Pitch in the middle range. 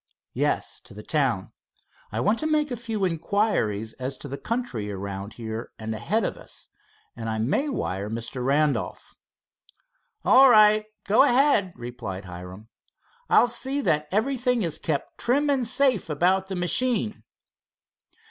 Yes: medium, 180 Hz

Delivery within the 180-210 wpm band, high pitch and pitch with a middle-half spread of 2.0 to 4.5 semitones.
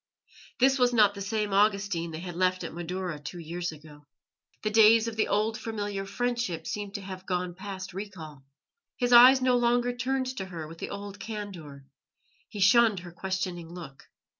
Yes: average, 185 wpm; high, 195 Hz; average, 4.1 semitones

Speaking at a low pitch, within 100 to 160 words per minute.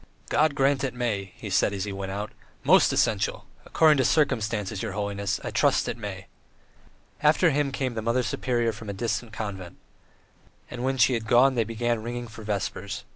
No: low, 115 Hz; average, 185 wpm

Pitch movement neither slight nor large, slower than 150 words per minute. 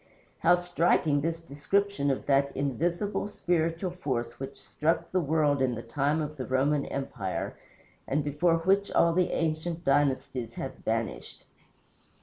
Yes: average, 3.7 semitones; average, 140 wpm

